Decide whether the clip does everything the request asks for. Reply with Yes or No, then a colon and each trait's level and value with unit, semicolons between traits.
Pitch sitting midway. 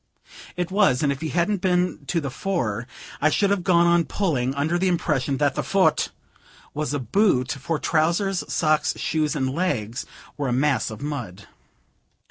Yes: medium, 155 Hz